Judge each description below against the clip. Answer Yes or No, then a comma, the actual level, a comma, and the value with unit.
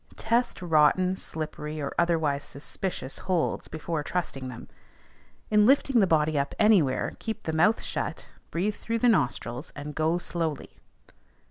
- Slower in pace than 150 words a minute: Yes, average, 140 wpm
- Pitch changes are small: No, average, 4.7 semitones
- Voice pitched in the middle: Yes, medium, 165 Hz